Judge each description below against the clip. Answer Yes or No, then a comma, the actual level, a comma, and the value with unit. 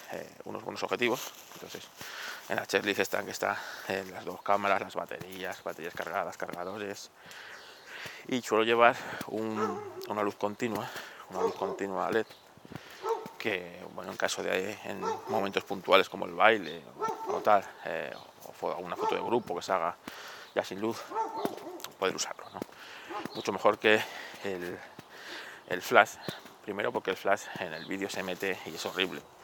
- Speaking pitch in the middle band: No, low, 115 Hz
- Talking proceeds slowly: No, average, 160 wpm